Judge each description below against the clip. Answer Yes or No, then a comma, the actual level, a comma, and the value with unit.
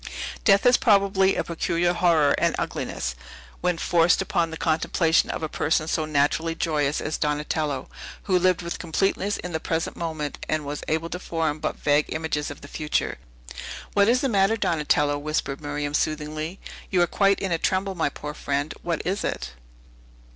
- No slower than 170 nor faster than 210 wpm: Yes, average, 175 wpm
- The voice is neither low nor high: Yes, medium, 160 Hz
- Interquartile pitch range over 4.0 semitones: No, average, 3.1 semitones